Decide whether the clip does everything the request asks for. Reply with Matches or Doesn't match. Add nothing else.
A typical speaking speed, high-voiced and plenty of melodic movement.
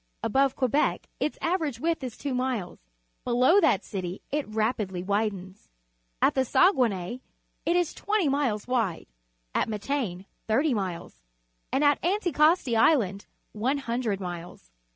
Doesn't match